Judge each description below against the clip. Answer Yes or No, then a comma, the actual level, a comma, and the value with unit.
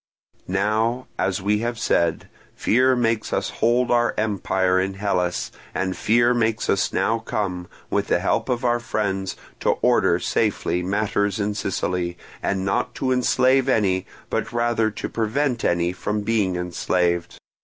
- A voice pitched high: No, low, 105 Hz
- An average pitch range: Yes, average, 4.1 semitones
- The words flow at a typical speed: Yes, average, 150 wpm